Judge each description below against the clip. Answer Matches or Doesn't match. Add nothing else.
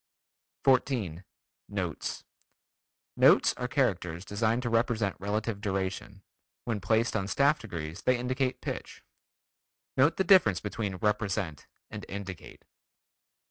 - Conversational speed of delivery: Doesn't match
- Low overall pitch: Matches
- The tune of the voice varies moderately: Matches